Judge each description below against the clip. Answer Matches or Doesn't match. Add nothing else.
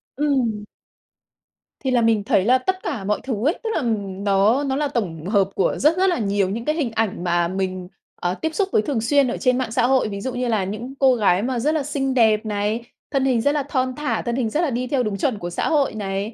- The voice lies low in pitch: Doesn't match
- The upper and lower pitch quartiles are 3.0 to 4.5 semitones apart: Doesn't match